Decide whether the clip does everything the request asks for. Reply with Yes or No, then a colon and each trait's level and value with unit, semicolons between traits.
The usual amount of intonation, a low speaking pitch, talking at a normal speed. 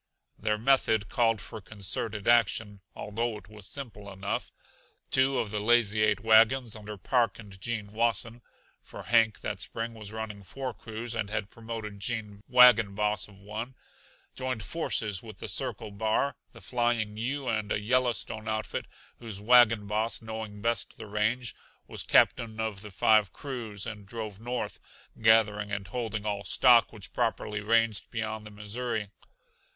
No: narrow, 2.2 semitones; low, 110 Hz; average, 155 wpm